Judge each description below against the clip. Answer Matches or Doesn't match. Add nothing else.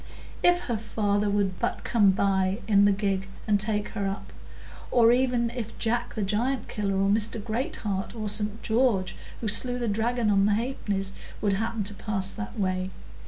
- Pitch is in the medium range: Doesn't match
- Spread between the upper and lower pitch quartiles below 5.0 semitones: Matches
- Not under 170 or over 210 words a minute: Matches